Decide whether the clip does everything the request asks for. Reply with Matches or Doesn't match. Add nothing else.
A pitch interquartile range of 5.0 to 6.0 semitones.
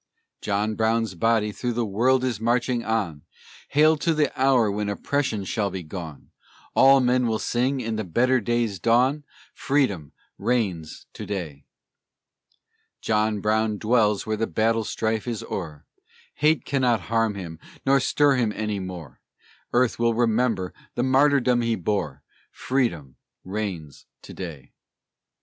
Doesn't match